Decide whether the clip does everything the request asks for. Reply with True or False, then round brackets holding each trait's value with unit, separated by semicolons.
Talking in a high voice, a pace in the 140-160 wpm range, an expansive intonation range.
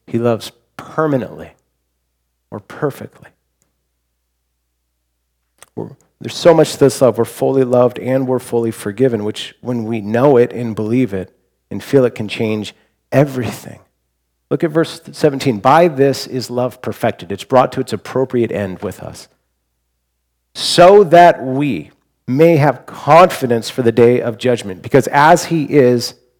False (120 Hz; 145 wpm; 5.9 semitones)